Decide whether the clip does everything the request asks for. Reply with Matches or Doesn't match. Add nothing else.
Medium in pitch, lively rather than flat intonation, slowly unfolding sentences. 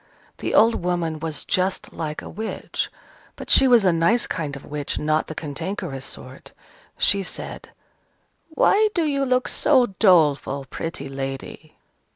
Doesn't match